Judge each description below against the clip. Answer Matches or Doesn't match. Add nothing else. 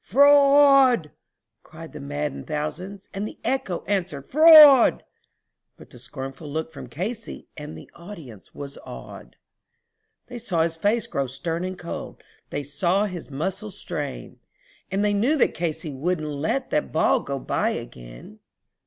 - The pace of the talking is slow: Doesn't match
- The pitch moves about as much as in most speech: Doesn't match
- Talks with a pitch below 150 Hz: Doesn't match